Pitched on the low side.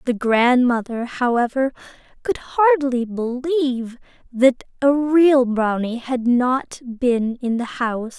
No: very high, 250 Hz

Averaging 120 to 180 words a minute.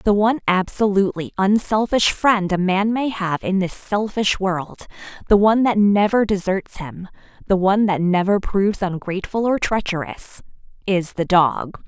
Yes: average, 150 wpm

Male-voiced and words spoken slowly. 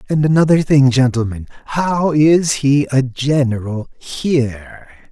Yes: male; slow, 115 wpm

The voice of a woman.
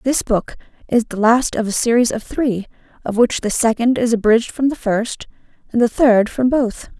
Yes: female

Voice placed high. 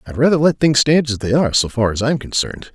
No: low, 130 Hz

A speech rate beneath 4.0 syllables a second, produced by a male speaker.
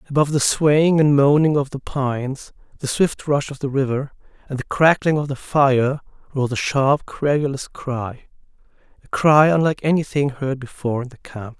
No: 5.0 syllables/s; male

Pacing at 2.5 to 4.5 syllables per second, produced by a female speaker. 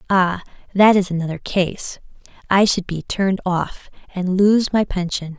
Yes: 4.3 syllables/s; female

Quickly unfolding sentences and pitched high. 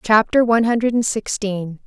No: slow, 130 wpm; high, 215 Hz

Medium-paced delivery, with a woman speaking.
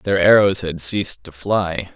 No: average, 185 wpm; male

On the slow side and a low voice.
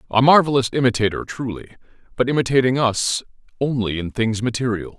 Yes: slow, 130 wpm; low, 120 Hz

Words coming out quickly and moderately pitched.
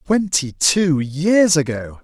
No: slow, 120 wpm; medium, 160 Hz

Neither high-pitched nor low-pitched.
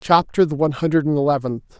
Yes: medium, 145 Hz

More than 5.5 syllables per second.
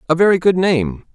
Yes: 5.7 syllables/s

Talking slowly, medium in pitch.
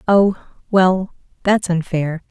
Yes: slow, 105 wpm; medium, 180 Hz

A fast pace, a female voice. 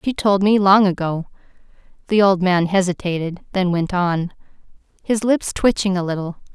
No: average, 155 wpm; female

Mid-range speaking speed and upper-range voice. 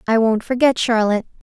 Yes: average, 160 wpm; high, 230 Hz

